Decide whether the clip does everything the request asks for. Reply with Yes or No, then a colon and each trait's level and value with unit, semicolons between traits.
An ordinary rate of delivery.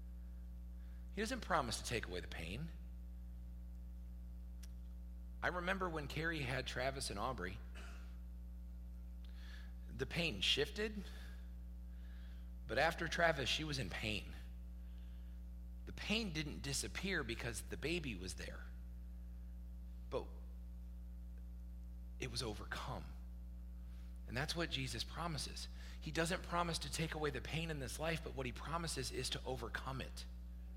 No: slow, 125 wpm